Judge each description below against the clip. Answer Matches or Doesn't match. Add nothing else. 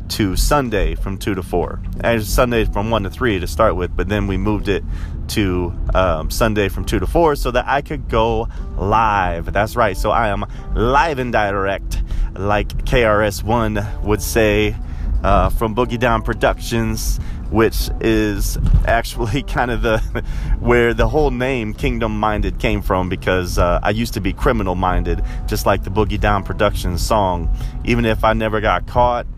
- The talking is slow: Doesn't match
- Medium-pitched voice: Doesn't match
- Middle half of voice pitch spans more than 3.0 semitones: Matches